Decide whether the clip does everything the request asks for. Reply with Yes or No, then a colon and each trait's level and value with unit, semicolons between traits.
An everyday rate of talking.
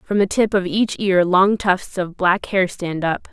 No: fast, 235 wpm